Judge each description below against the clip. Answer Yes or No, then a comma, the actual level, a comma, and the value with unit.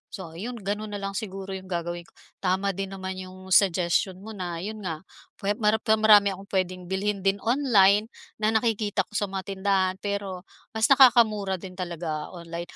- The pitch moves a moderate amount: No, narrow, 2.2 semitones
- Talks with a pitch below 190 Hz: No, high, 195 Hz